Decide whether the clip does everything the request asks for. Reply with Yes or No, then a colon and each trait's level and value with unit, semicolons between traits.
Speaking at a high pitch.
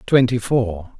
No: low, 115 Hz